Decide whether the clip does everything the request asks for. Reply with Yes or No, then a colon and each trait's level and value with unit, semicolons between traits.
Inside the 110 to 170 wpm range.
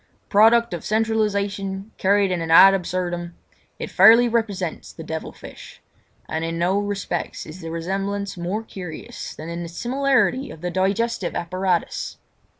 Yes: average, 150 wpm